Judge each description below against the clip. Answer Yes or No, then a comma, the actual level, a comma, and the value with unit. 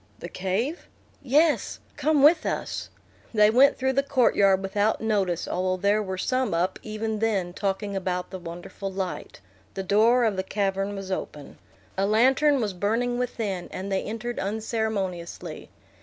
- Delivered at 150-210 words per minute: Yes, average, 155 wpm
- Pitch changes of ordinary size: Yes, average, 3.8 semitones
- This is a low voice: No, high, 205 Hz